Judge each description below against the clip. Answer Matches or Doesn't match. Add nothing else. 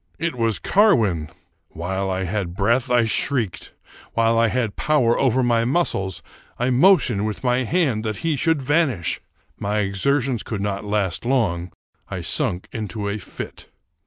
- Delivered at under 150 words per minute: Doesn't match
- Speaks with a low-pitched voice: Matches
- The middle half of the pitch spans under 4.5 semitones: Doesn't match